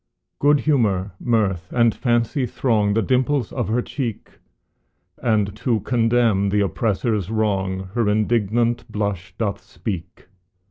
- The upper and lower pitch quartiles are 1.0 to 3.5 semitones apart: Yes, average, 3.1 semitones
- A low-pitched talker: Yes, low, 110 Hz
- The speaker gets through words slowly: Yes, slow, 125 wpm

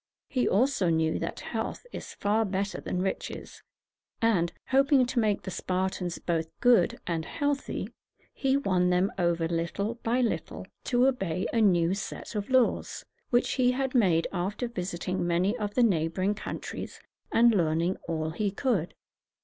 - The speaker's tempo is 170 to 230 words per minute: No, average, 155 wpm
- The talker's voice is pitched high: Yes, high, 195 Hz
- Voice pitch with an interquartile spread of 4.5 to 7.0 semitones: Yes, wide, 5.6 semitones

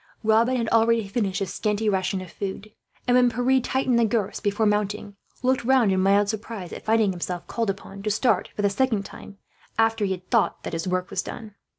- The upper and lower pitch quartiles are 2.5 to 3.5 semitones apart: Yes, average, 2.8 semitones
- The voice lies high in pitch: Yes, high, 210 Hz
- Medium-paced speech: No, fast, 215 wpm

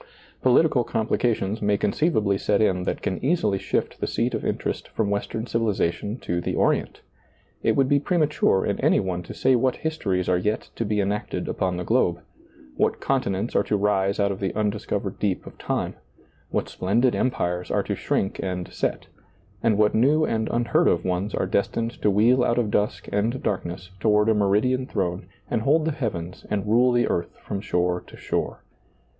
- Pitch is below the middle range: Yes, low, 105 Hz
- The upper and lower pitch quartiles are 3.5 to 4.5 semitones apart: Yes, average, 4.0 semitones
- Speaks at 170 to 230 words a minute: Yes, average, 195 wpm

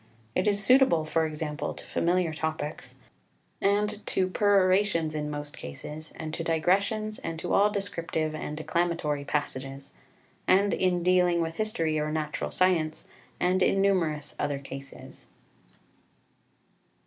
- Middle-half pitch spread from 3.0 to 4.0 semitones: Yes, average, 3.7 semitones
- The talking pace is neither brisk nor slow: No, slow, 130 wpm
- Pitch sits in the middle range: Yes, medium, 165 Hz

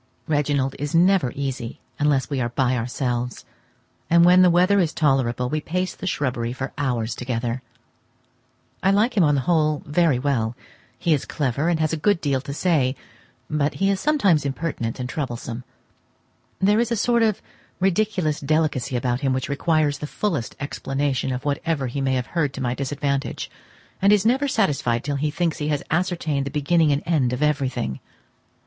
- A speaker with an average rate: Yes, average, 180 wpm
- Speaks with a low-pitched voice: No, medium, 145 Hz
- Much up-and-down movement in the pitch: No, average, 4.7 semitones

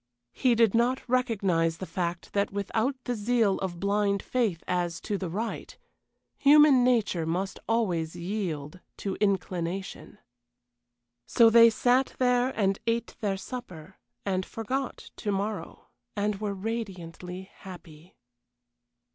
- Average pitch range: Yes, average, 4.3 semitones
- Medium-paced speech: No, slow, 125 wpm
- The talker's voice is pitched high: Yes, high, 200 Hz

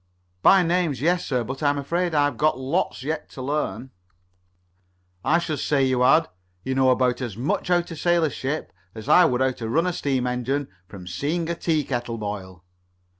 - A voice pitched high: No, medium, 140 Hz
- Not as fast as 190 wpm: No, average, 195 wpm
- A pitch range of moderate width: Yes, average, 4.5 semitones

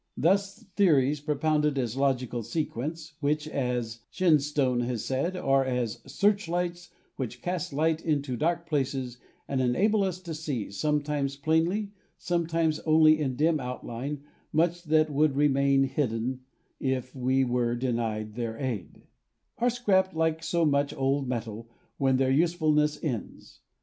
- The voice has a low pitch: No, medium, 145 Hz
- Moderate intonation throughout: Yes, average, 4.1 semitones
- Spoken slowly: No, average, 145 wpm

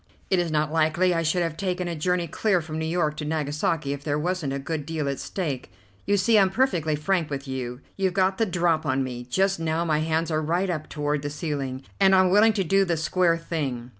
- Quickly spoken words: Yes, fast, 235 wpm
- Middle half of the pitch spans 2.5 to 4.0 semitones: Yes, average, 3.6 semitones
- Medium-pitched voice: Yes, medium, 160 Hz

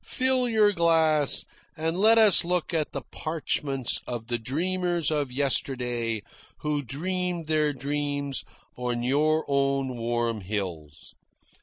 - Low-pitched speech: No, medium, 145 Hz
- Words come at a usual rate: No, slow, 125 wpm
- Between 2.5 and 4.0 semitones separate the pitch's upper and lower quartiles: No, average, 5.3 semitones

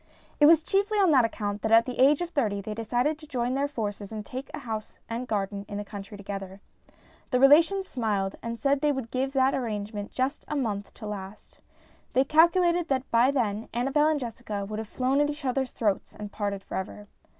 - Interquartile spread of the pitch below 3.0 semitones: No, average, 5.2 semitones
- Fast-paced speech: Yes, fast, 215 wpm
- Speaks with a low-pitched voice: No, high, 240 Hz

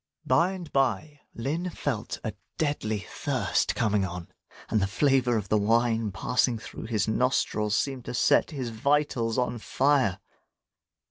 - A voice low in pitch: Yes, low, 120 Hz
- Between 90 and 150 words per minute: Yes, average, 145 wpm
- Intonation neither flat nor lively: Yes, average, 4.5 semitones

